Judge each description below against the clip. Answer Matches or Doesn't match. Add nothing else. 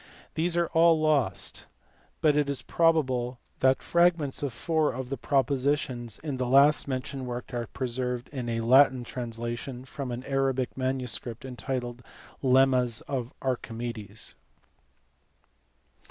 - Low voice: Matches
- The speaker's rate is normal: Doesn't match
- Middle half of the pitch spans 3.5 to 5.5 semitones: Doesn't match